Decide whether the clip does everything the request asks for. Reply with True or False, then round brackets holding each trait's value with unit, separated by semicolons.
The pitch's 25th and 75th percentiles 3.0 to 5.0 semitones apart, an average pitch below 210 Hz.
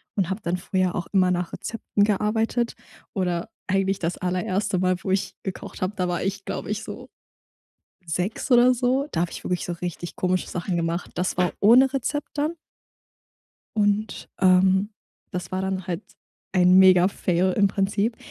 False (2.5 semitones; 190 Hz)